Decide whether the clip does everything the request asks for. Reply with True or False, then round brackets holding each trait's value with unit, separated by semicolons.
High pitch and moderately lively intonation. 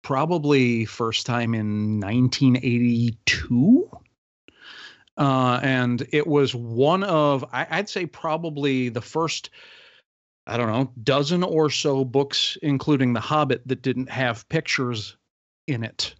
False (130 Hz; 3.6 semitones)